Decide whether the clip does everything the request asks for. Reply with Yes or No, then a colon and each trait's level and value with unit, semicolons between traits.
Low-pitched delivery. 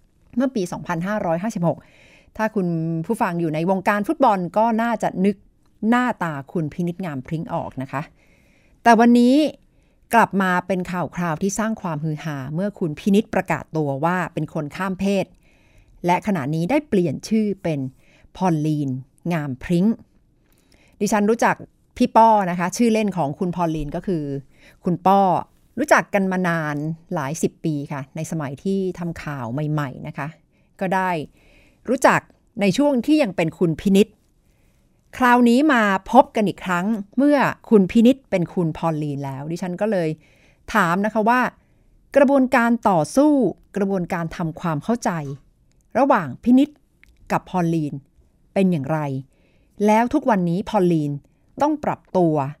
No: medium, 180 Hz